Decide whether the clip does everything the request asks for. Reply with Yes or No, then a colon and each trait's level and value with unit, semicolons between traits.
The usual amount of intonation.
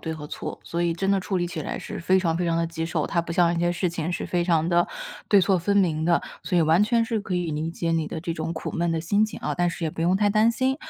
No: narrow, 2.3 semitones